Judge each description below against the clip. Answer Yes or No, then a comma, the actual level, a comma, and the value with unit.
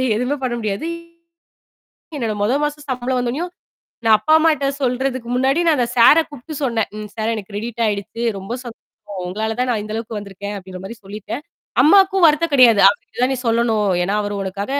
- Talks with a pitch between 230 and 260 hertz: Yes, high, 235 Hz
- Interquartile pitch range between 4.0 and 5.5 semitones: Yes, average, 4.3 semitones